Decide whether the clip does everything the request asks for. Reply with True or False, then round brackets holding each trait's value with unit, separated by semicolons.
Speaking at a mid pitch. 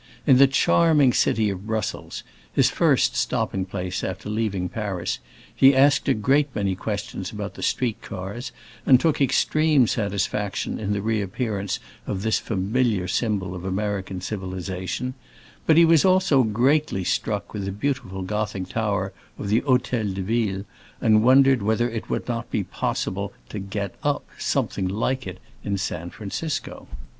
False (105 Hz)